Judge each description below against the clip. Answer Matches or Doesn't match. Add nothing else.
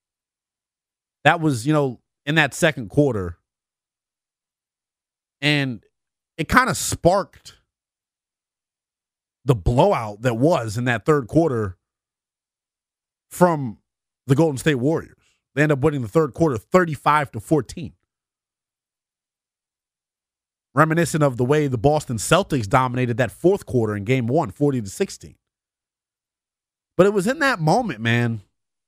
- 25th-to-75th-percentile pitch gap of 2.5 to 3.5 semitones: Doesn't match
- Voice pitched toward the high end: Doesn't match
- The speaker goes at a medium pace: Doesn't match